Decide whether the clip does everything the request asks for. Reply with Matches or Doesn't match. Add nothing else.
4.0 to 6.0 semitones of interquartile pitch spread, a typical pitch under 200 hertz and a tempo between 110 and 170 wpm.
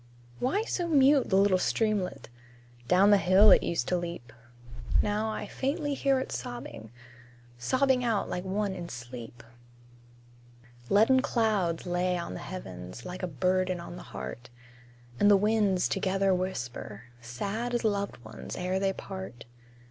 Matches